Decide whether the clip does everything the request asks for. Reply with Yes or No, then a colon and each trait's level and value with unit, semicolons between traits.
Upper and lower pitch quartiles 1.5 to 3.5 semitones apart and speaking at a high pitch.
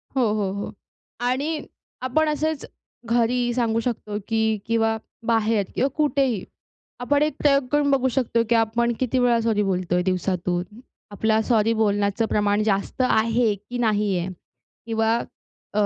Yes: average, 3.1 semitones; high, 225 Hz